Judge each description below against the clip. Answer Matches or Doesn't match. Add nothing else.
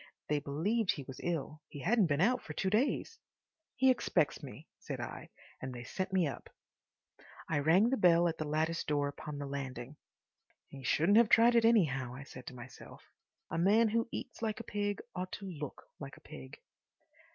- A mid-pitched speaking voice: Matches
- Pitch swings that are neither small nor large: Doesn't match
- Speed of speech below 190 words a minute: Doesn't match